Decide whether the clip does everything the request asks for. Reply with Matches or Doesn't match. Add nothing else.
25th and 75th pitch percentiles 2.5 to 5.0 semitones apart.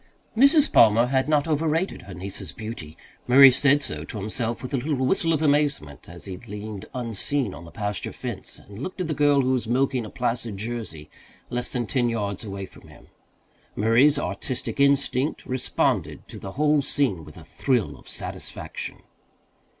Doesn't match